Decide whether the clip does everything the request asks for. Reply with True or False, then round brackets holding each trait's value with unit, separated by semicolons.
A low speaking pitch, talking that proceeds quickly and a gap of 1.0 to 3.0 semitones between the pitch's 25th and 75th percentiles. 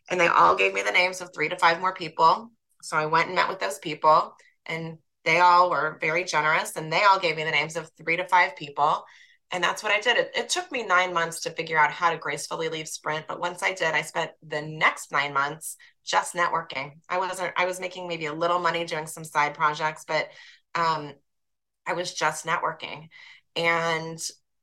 False (165 Hz; 220 wpm; 2.5 semitones)